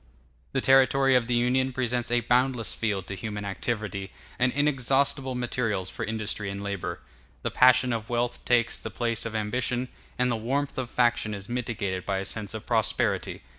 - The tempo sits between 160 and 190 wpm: Yes, average, 180 wpm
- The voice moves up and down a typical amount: Yes, average, 3.2 semitones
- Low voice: Yes, low, 120 Hz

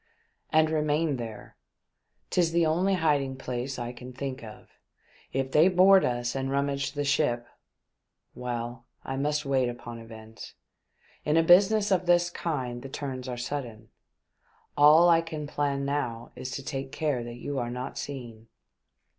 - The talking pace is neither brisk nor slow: Yes, average, 165 wpm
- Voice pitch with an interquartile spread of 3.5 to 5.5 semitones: Yes, average, 4.2 semitones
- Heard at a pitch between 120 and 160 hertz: Yes, medium, 140 Hz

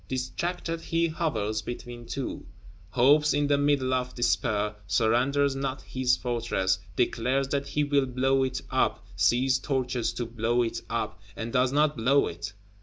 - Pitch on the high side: No, low, 130 Hz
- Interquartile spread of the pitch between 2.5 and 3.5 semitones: Yes, average, 3.2 semitones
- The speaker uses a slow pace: No, average, 155 wpm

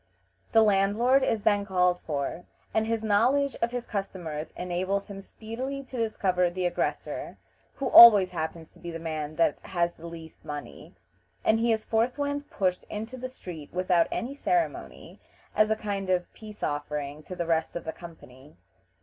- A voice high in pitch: Yes, high, 195 Hz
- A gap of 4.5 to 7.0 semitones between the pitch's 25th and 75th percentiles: Yes, average, 5.0 semitones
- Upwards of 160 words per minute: Yes, average, 170 wpm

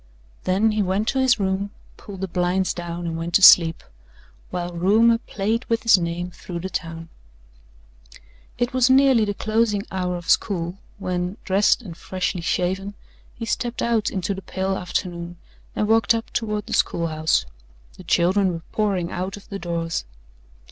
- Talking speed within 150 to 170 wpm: Yes, average, 165 wpm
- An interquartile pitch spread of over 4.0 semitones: No, average, 3.5 semitones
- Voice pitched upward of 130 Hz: Yes, high, 190 Hz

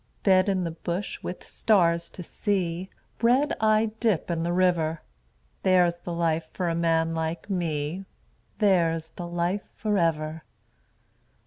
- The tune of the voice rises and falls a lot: No, average, 2.7 semitones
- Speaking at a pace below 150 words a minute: Yes, average, 140 wpm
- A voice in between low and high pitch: Yes, medium, 175 Hz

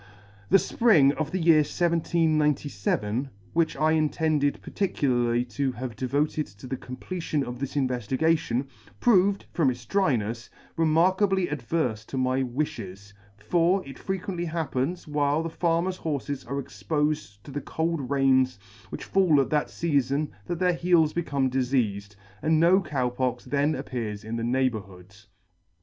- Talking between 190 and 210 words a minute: No, average, 140 wpm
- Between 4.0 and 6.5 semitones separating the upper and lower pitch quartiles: Yes, average, 4.7 semitones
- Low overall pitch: No, medium, 145 Hz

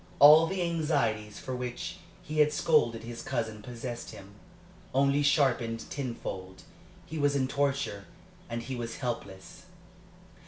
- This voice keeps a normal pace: No, slow, 130 wpm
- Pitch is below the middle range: Yes, low, 125 Hz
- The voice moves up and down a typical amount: Yes, average, 3.9 semitones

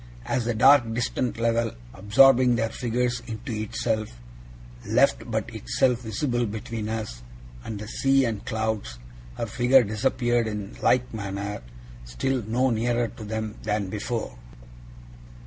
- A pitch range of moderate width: No, narrow, 2.3 semitones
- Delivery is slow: Yes, slow, 130 wpm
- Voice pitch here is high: No, low, 115 Hz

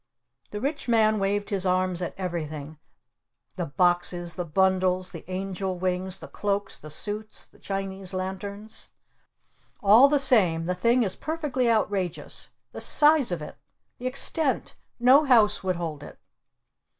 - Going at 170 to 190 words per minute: No, average, 145 wpm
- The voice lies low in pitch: No, high, 190 Hz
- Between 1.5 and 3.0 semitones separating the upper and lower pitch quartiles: No, average, 3.5 semitones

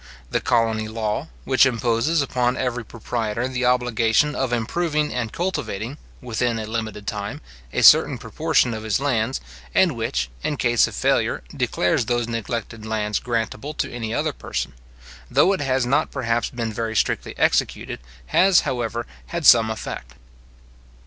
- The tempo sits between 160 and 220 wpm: No, average, 150 wpm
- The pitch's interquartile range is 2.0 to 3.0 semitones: Yes, average, 2.7 semitones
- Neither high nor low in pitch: No, low, 120 Hz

